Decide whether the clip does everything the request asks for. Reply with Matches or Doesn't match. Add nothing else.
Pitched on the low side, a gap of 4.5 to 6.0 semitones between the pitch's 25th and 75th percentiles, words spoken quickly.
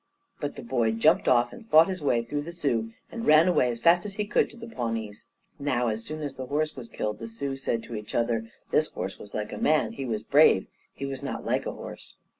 Matches